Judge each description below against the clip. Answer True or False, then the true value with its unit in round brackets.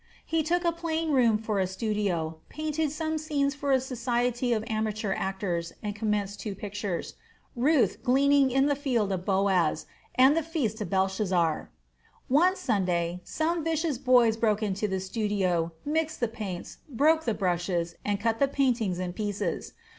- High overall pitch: True (220 Hz)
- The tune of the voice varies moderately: False (6.5 semitones)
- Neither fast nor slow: True (160 wpm)